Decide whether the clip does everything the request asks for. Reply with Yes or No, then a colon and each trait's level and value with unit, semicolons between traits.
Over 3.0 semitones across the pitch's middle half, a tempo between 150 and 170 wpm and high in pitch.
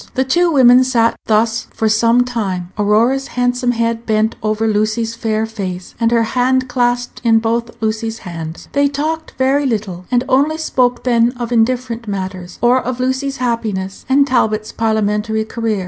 No: average, 2.7 semitones; average, 160 wpm; high, 230 Hz